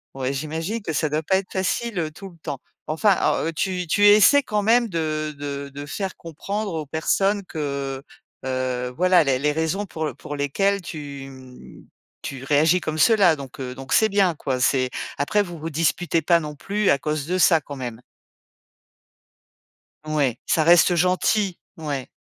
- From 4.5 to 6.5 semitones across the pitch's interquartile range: Yes, average, 4.9 semitones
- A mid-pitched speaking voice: Yes, medium, 155 Hz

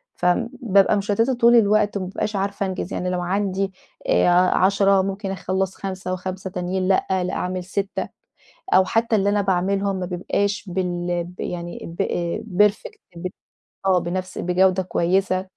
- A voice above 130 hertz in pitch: Yes, high, 190 Hz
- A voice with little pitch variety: Yes, narrow, 1.7 semitones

